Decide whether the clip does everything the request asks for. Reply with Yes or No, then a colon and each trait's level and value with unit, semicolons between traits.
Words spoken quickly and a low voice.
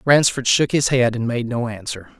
Yes: fast, 220 wpm; low, 125 Hz